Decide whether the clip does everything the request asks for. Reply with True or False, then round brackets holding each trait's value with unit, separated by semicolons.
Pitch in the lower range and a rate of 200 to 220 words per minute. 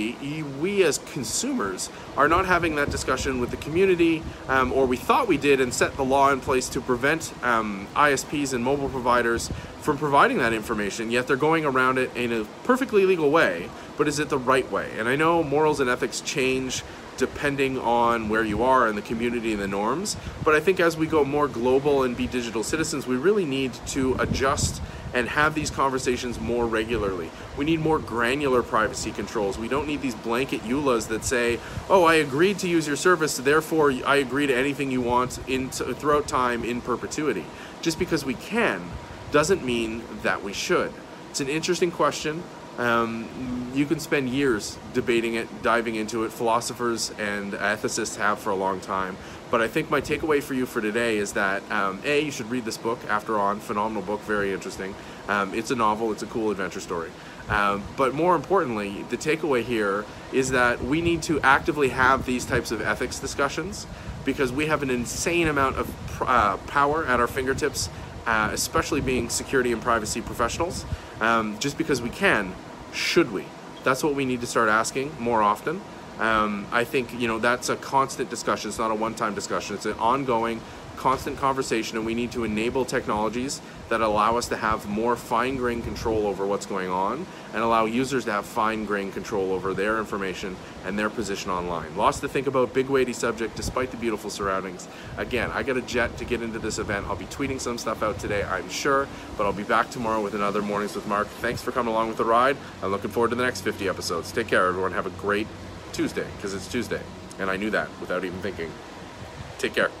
True (120 Hz; 205 wpm)